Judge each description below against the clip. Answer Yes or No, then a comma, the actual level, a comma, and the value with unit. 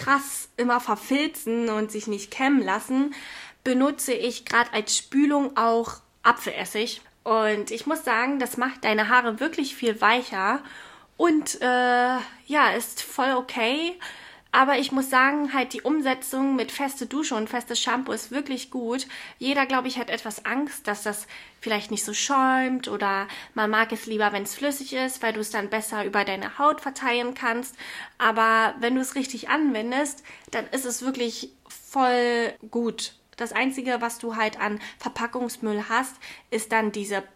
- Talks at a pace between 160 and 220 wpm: Yes, average, 165 wpm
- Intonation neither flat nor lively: Yes, average, 3.2 semitones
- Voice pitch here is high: Yes, high, 245 Hz